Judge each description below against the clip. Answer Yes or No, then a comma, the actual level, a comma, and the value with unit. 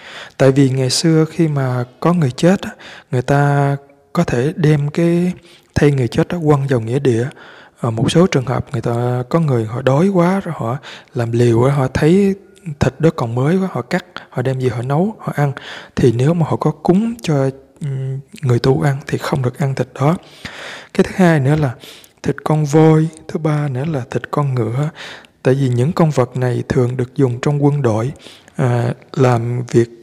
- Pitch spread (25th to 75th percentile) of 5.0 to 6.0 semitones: No, average, 4.2 semitones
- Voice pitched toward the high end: No, medium, 140 Hz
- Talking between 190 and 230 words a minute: Yes, average, 200 wpm